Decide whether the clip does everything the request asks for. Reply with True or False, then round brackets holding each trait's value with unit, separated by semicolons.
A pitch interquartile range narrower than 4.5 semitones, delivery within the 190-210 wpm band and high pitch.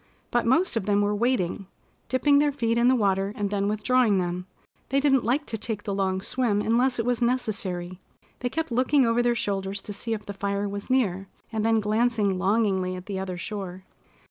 True (3.8 semitones; 205 wpm; 210 Hz)